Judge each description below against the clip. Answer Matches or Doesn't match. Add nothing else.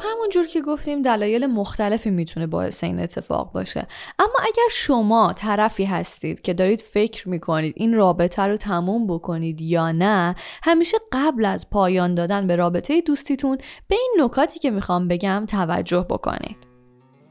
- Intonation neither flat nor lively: Doesn't match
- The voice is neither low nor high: Doesn't match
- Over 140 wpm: Matches